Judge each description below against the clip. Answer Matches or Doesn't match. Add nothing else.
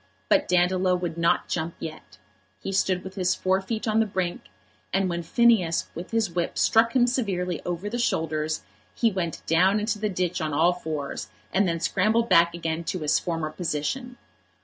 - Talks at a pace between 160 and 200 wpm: Matches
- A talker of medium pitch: Matches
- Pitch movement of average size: Matches